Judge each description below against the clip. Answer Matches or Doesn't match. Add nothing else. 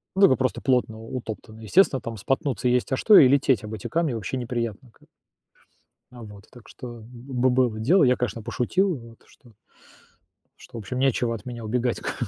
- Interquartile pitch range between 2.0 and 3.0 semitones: Matches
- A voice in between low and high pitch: Doesn't match